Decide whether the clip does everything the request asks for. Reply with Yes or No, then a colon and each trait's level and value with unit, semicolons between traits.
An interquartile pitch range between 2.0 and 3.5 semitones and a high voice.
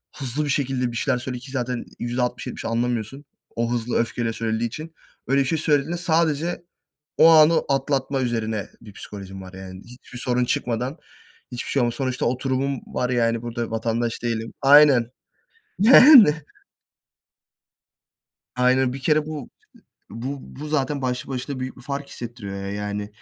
No: average, 3.1 semitones; low, 125 Hz